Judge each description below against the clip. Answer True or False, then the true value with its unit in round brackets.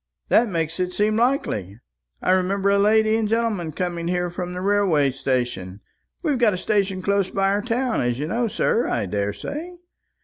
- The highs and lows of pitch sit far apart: False (5.0 semitones)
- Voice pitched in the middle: False (195 Hz)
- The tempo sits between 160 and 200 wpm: True (180 wpm)